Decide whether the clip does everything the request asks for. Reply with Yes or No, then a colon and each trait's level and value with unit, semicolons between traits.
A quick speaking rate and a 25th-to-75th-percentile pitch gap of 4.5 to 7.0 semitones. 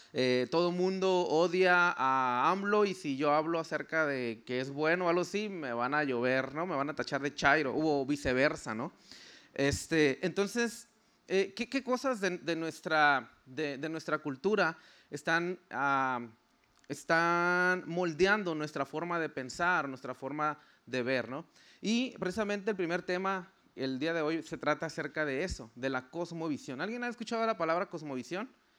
No: average, 170 wpm; average, 4.8 semitones